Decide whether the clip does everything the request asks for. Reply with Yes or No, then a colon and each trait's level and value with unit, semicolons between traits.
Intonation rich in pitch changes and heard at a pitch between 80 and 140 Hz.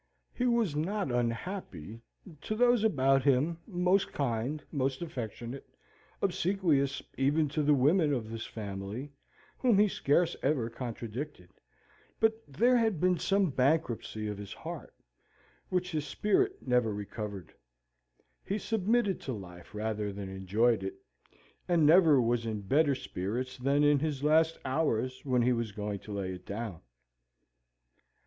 Yes: wide, 7.4 semitones; low, 135 Hz